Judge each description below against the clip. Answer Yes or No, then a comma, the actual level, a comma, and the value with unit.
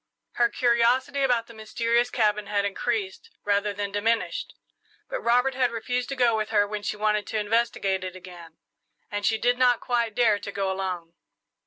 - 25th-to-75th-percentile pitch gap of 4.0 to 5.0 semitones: No, average, 3.0 semitones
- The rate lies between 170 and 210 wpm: Yes, average, 180 wpm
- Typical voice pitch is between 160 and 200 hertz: No, high, 220 Hz